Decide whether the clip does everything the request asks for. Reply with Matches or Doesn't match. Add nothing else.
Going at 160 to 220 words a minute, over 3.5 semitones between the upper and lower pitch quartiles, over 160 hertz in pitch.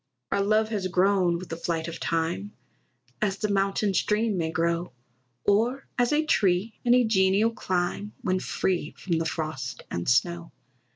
Matches